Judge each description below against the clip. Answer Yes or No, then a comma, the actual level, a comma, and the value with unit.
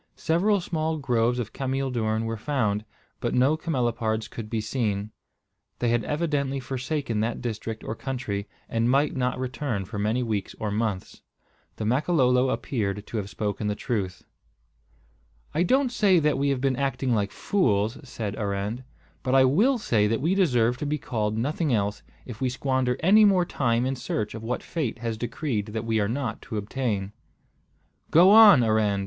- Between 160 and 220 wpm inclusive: Yes, average, 175 wpm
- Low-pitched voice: Yes, low, 120 Hz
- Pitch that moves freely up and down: No, average, 4.4 semitones